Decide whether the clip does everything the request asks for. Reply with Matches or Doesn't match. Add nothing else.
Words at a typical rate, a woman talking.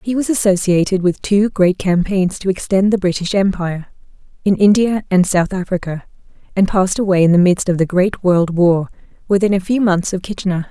Matches